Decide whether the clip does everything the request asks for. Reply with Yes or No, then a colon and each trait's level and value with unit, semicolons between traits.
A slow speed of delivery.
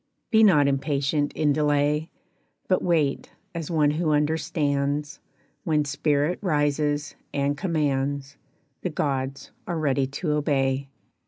Yes: slow, 115 wpm